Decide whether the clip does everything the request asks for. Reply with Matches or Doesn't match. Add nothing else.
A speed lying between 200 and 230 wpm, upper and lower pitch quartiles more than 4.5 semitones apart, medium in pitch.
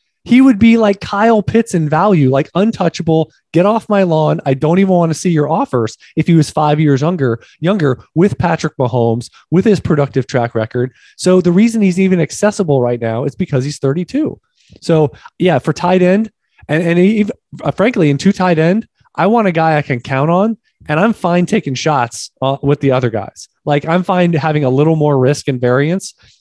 Matches